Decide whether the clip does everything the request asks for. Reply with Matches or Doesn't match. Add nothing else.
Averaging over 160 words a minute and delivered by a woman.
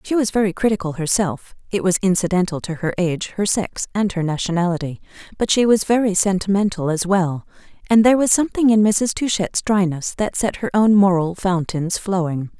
Matches